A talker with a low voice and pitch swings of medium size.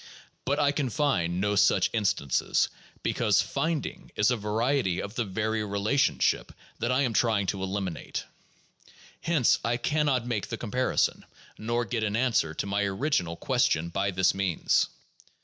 Yes: low, 110 Hz; average, 4.5 semitones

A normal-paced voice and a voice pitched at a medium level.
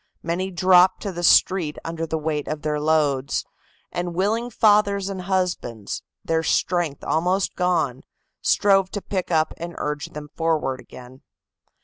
Yes: average, 145 wpm; medium, 170 Hz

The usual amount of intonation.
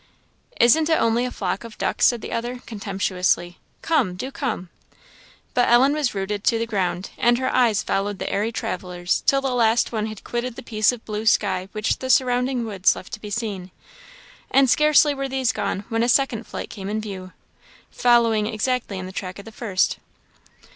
Yes: average, 3.8 semitones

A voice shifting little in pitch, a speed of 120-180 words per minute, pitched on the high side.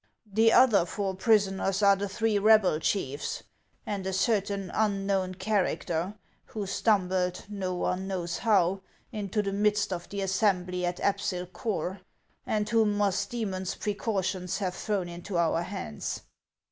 Yes: narrow, 2.3 semitones; slow, 135 wpm; high, 195 Hz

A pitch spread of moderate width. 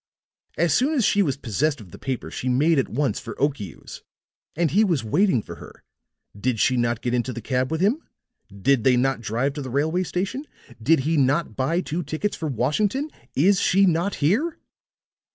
No: wide, 6.2 semitones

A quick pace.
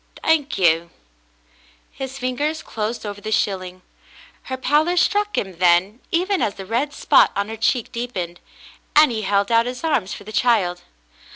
No: average, 165 wpm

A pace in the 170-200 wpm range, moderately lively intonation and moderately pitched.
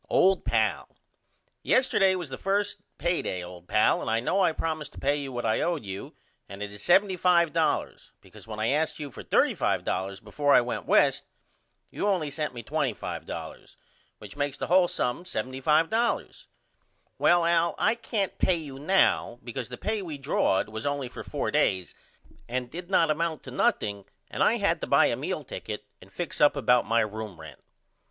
No: average, 185 wpm; wide, 7.5 semitones; medium, 145 Hz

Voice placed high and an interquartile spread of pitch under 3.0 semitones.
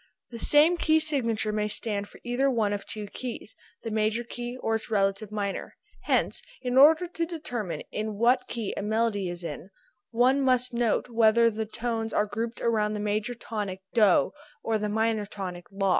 Yes: high, 225 Hz; narrow, 2.6 semitones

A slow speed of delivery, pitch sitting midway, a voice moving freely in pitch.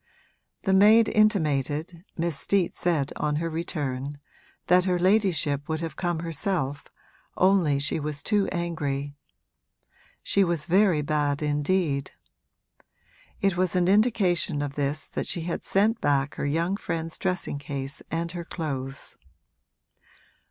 No: slow, 130 wpm; medium, 165 Hz; average, 4.2 semitones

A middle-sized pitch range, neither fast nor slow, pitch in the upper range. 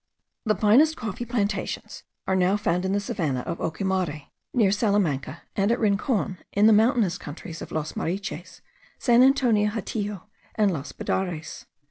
Yes: average, 3.7 semitones; average, 150 wpm; high, 200 Hz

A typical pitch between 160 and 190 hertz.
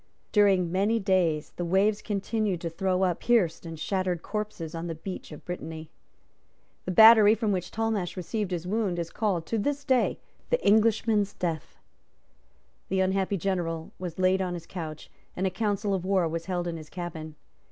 Yes: medium, 185 Hz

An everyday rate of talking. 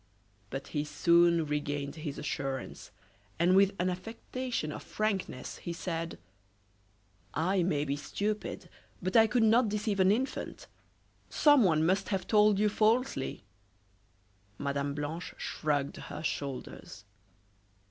No: slow, 120 wpm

